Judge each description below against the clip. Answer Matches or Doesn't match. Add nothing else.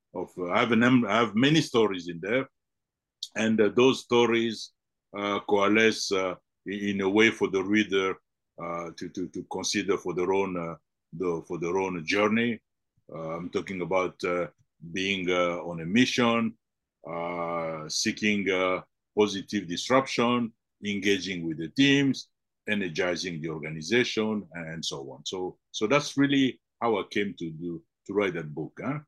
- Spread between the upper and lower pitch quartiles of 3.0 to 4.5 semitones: Doesn't match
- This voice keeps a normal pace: Matches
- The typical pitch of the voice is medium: Doesn't match